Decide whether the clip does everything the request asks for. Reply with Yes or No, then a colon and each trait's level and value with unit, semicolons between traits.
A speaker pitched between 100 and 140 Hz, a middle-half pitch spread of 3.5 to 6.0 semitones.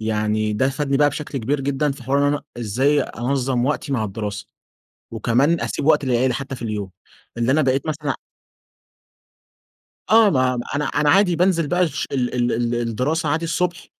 Yes: low, 135 Hz; average, 3.8 semitones